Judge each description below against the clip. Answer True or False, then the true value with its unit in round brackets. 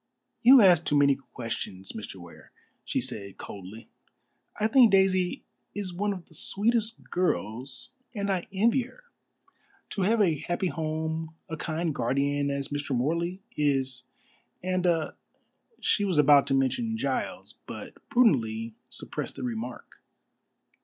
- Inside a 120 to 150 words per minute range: True (145 wpm)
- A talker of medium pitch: True (160 Hz)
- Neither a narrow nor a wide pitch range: False (6.4 semitones)